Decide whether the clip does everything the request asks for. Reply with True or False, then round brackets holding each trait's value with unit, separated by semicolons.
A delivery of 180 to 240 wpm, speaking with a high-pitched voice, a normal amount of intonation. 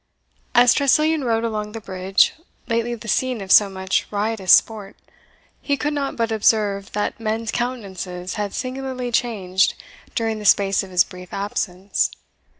False (155 wpm; 215 Hz; 3.6 semitones)